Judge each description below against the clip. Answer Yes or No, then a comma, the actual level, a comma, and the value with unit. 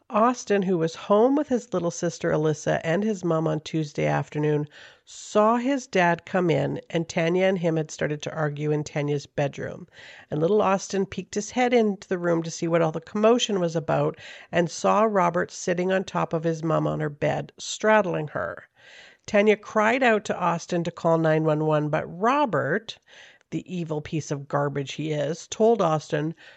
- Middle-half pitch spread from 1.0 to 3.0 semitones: No, average, 4.8 semitones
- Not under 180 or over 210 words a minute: Yes, average, 185 wpm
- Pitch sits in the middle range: Yes, medium, 170 Hz